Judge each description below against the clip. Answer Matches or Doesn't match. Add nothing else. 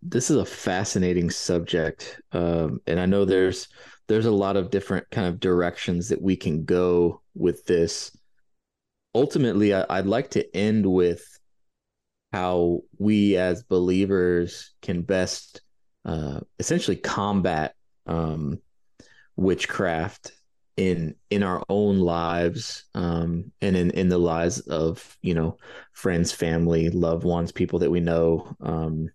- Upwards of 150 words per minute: Doesn't match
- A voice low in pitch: Matches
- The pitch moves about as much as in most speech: Doesn't match